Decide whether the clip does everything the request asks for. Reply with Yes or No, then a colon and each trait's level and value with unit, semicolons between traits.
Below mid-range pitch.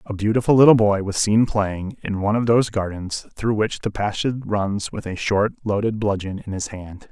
Yes: low, 105 Hz